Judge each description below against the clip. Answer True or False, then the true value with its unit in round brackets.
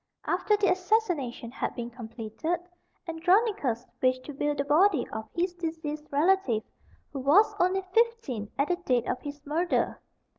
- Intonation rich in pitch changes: True (6.2 semitones)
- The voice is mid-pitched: False (305 Hz)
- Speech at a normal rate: True (150 wpm)